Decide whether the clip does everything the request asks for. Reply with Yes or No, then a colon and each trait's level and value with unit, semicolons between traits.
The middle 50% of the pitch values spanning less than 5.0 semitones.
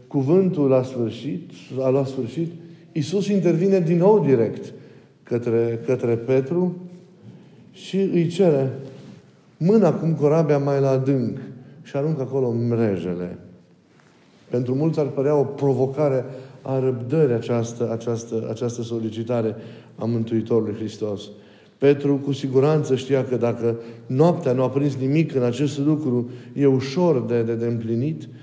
Yes: average, 4.3 semitones